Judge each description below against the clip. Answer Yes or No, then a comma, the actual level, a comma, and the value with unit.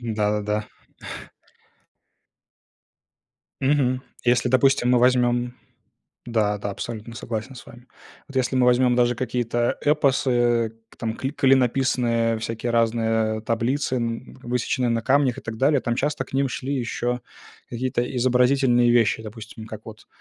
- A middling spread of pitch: No, narrow, 2.1 semitones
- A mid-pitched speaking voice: No, low, 120 Hz